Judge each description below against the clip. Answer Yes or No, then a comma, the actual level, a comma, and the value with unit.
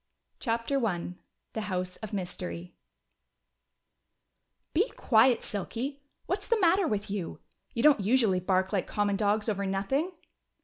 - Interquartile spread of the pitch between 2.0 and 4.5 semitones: No, wide, 5.5 semitones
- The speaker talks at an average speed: No, slow, 130 wpm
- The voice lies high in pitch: Yes, high, 210 Hz